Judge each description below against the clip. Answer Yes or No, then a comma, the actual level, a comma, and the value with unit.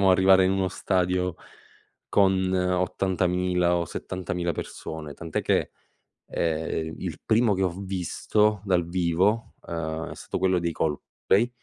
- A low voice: Yes, very low, 90 Hz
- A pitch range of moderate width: No, narrow, 1.9 semitones